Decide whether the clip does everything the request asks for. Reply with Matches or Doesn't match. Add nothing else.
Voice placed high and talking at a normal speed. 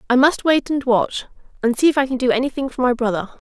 Doesn't match